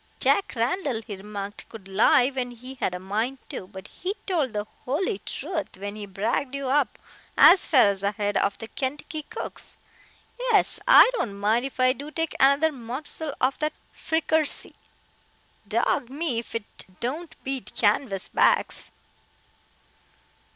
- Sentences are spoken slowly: No, average, 150 wpm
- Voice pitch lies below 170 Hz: No, very high, 255 Hz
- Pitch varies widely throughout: Yes, wide, 6.2 semitones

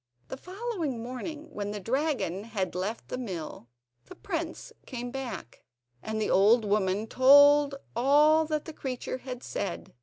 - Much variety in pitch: Yes, wide, 5.9 semitones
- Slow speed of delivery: No, average, 155 wpm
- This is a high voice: Yes, very high, 255 Hz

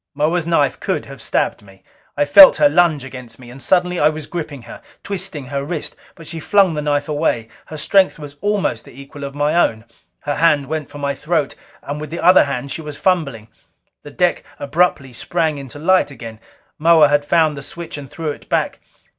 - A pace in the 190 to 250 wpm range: Yes, fast, 205 wpm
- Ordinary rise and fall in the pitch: Yes, average, 3.2 semitones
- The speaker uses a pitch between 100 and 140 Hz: No, medium, 150 Hz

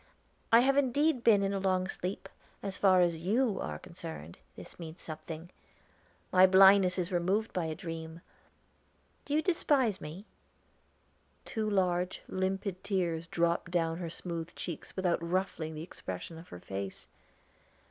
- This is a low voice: No, medium, 180 Hz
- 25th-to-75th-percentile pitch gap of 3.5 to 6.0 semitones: No, average, 3.0 semitones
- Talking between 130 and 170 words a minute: Yes, average, 145 wpm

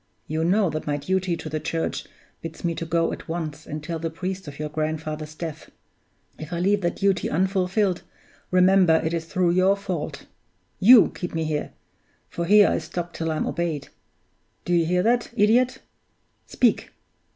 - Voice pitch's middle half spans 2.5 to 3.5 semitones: Yes, average, 3.1 semitones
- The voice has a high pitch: No, medium, 170 Hz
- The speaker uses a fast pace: No, average, 175 wpm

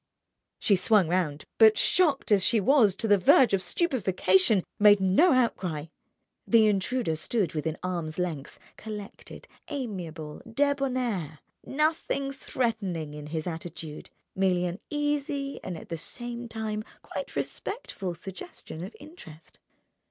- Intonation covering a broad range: Yes, wide, 6.5 semitones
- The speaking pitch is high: Yes, high, 200 Hz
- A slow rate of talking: Yes, slow, 130 wpm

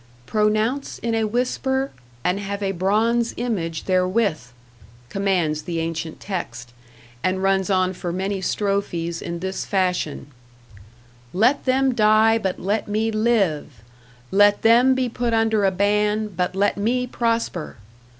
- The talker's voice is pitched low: No, high, 200 Hz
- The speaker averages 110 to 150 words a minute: Yes, slow, 135 wpm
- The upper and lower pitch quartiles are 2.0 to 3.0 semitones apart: No, average, 3.7 semitones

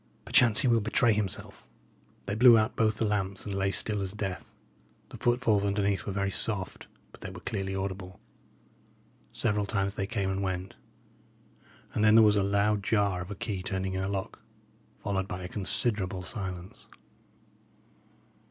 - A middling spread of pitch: No, narrow, 1.9 semitones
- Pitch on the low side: Yes, low, 100 Hz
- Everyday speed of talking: Yes, average, 170 wpm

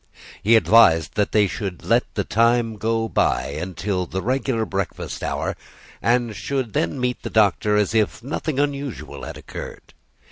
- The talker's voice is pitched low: Yes, low, 110 Hz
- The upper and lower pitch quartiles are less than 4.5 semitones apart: Yes, average, 3.7 semitones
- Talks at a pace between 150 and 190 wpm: Yes, average, 155 wpm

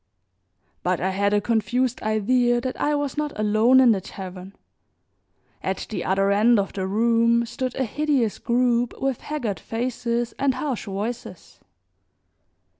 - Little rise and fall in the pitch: No, average, 3.7 semitones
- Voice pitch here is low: No, high, 235 Hz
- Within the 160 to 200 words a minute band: No, average, 145 wpm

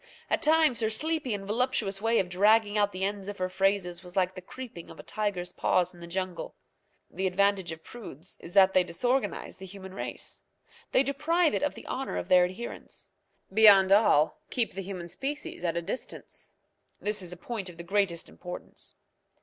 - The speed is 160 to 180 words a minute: No, average, 195 wpm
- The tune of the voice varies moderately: Yes, average, 3.8 semitones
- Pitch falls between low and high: No, high, 195 Hz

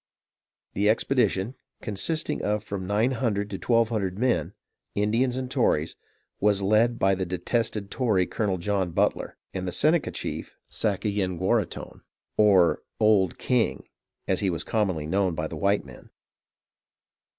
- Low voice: Yes, low, 105 Hz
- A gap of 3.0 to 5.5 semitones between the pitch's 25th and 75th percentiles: Yes, average, 3.4 semitones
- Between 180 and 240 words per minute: No, average, 140 wpm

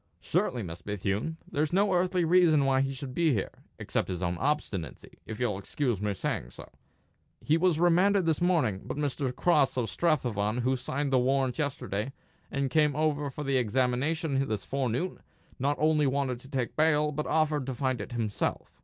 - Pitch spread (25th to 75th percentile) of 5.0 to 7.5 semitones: No, average, 4.1 semitones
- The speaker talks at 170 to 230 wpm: Yes, average, 180 wpm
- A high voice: No, low, 135 Hz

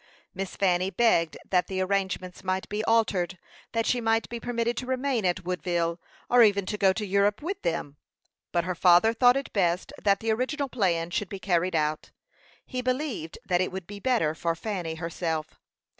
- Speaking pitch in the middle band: No, high, 195 Hz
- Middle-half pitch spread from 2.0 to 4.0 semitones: No, average, 4.5 semitones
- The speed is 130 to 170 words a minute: No, average, 190 wpm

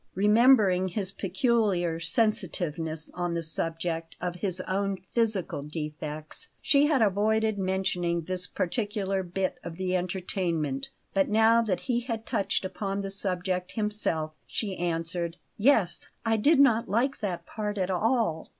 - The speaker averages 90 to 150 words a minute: Yes, average, 140 wpm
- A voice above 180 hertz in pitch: Yes, high, 190 Hz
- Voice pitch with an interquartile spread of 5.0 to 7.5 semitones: No, average, 4.0 semitones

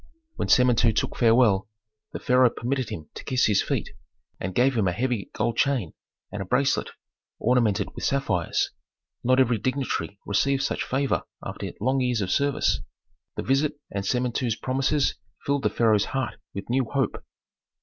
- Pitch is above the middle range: No, low, 125 Hz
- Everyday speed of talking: Yes, average, 160 wpm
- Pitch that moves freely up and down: No, average, 3.8 semitones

